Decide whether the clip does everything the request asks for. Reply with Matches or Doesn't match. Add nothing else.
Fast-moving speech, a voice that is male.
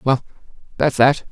Doesn't match